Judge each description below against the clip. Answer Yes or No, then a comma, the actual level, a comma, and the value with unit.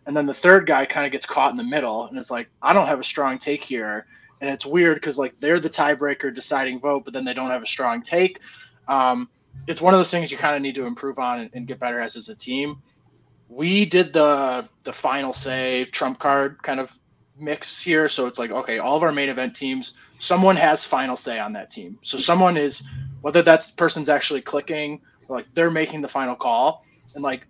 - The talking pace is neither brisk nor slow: No, fast, 230 wpm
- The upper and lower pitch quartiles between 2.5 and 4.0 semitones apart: Yes, average, 3.3 semitones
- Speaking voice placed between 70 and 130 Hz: No, medium, 140 Hz